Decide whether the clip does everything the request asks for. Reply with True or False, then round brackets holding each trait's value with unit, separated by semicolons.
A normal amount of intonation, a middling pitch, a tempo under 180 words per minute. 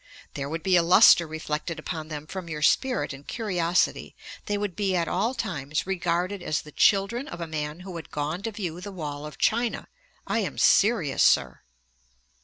False (4.3 semitones; 175 Hz; 190 wpm)